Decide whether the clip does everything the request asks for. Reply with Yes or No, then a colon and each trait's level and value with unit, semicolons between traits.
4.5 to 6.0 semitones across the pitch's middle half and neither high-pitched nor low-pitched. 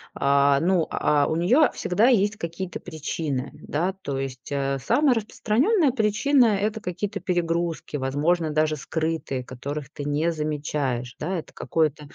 Yes: wide, 5.4 semitones; medium, 160 Hz